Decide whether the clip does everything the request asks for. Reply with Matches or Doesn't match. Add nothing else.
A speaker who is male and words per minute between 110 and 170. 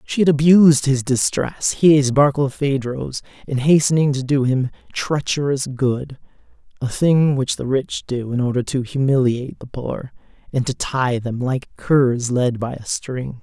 Matches